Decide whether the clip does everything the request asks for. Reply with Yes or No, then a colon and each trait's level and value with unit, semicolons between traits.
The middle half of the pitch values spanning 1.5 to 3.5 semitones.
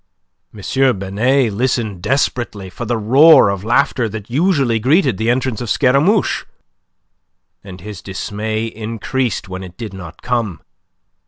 No: average, 4.5 semitones